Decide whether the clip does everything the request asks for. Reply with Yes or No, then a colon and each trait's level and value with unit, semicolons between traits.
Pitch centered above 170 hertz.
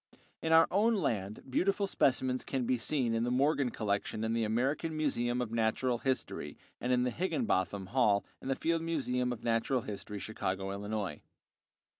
No: low, 125 Hz